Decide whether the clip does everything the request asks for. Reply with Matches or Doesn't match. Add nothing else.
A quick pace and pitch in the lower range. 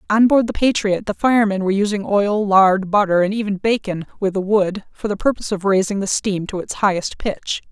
Doesn't match